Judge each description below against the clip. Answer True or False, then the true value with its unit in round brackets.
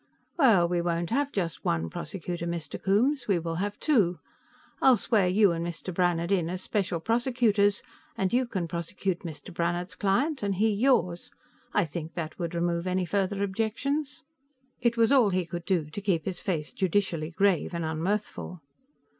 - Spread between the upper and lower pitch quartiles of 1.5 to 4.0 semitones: True (3.6 semitones)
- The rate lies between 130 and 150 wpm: False (170 wpm)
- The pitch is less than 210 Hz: True (185 Hz)